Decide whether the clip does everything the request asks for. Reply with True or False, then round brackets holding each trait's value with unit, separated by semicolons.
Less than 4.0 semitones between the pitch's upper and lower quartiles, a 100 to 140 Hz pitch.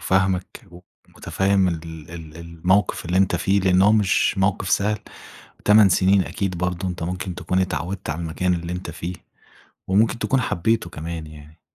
False (2.4 semitones; 90 Hz)